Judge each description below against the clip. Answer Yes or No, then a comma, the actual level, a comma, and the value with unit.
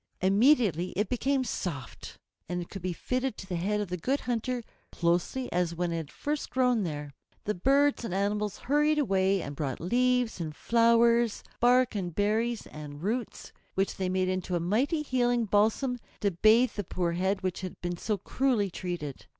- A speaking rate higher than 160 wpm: Yes, average, 180 wpm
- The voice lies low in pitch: No, high, 205 Hz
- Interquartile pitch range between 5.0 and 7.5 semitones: Yes, wide, 5.5 semitones